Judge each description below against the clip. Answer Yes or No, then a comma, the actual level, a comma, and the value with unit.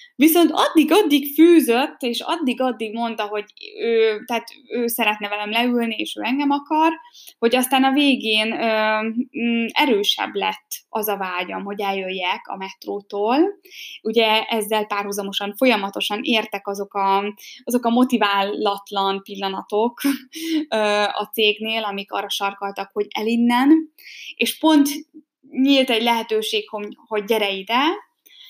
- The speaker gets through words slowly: No, average, 125 wpm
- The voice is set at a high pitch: Yes, high, 230 Hz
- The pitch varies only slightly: No, average, 5.2 semitones